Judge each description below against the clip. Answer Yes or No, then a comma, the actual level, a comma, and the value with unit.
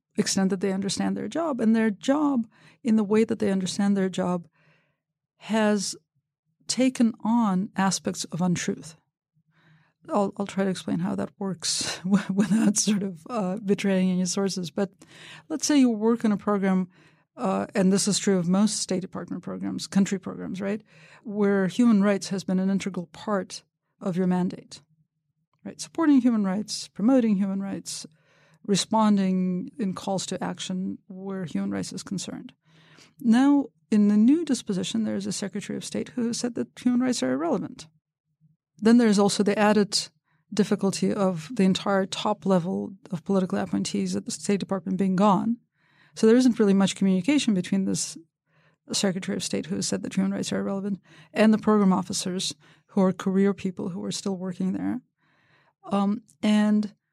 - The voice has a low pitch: No, high, 195 Hz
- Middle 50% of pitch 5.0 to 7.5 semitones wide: No, average, 3.0 semitones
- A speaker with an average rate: Yes, average, 170 wpm